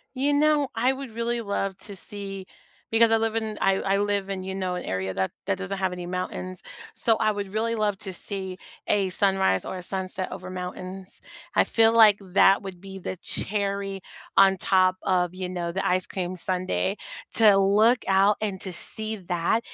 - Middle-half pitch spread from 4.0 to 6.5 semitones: No, narrow, 2.5 semitones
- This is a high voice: Yes, high, 195 Hz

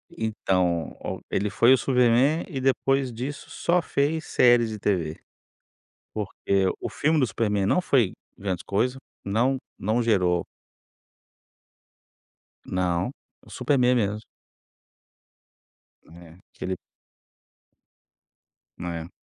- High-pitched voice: No, low, 110 Hz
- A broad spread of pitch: Yes, wide, 5.7 semitones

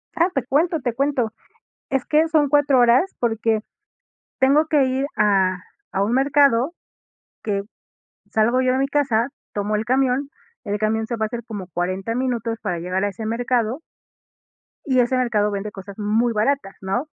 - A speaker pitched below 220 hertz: No, high, 235 Hz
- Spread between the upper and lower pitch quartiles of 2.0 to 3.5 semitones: No, average, 4.2 semitones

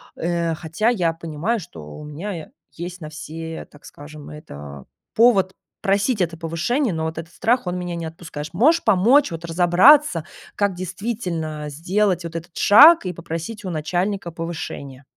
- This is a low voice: No, medium, 170 Hz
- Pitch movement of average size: Yes, average, 3.8 semitones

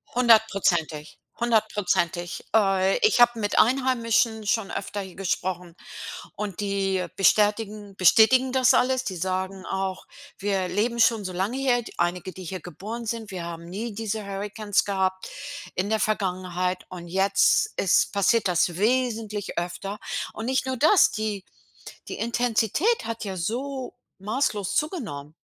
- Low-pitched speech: No, high, 205 Hz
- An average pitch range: Yes, average, 3.6 semitones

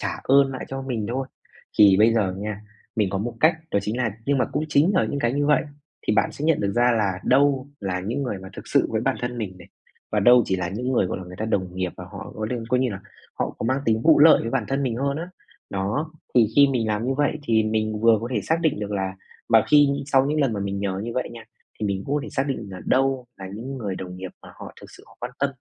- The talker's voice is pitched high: No, low, 115 Hz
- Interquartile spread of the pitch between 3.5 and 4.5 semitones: No, average, 5.0 semitones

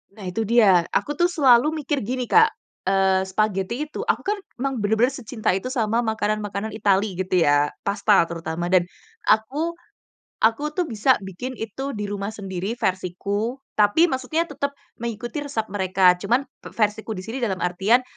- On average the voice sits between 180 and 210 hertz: No, high, 220 Hz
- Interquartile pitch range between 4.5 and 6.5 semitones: Yes, average, 4.9 semitones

